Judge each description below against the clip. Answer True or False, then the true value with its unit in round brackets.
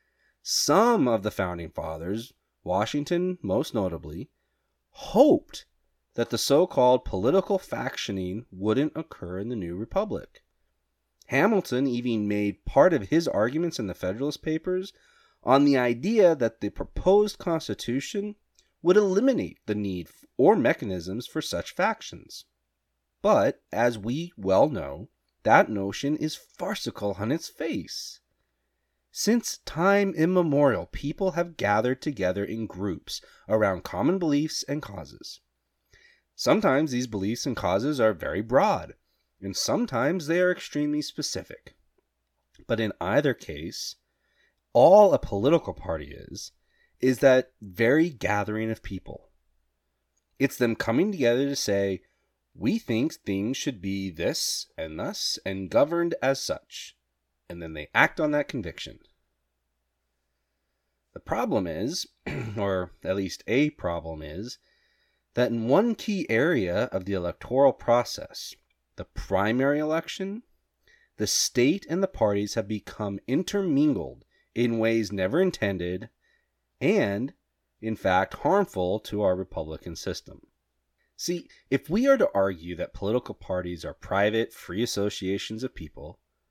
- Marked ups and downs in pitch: True (8.8 semitones)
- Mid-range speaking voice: False (110 Hz)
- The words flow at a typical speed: False (130 wpm)